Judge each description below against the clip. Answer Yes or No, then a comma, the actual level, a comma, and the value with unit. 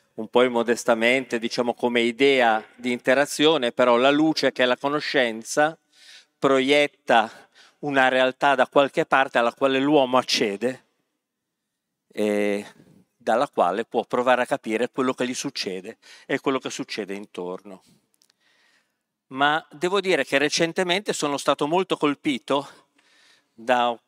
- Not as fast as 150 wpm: Yes, average, 130 wpm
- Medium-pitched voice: No, low, 130 Hz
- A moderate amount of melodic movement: Yes, average, 3.3 semitones